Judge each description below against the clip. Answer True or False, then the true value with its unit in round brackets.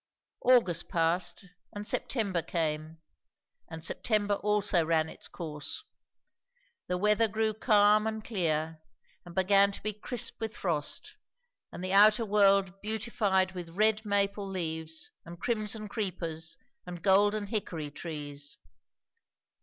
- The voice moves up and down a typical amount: True (4.2 semitones)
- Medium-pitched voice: False (195 Hz)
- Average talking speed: False (120 wpm)